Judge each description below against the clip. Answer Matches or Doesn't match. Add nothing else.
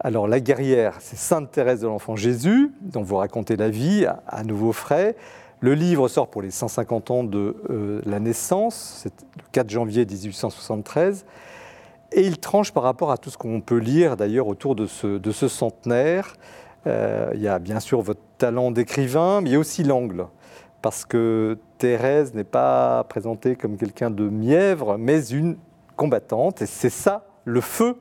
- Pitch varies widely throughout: Matches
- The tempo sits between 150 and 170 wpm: Doesn't match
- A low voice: Matches